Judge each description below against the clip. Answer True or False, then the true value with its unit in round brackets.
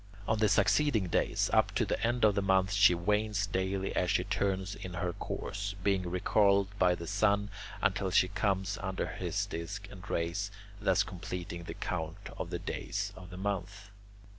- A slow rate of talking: False (180 wpm)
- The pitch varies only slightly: True (1.9 semitones)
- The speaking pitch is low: True (95 Hz)